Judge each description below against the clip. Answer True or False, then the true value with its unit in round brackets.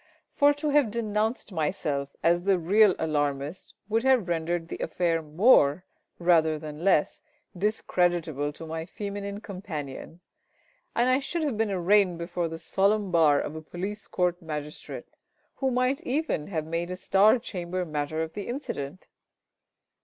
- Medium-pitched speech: True (180 Hz)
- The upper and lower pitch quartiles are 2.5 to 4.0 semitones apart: False (4.7 semitones)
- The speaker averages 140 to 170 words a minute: True (150 wpm)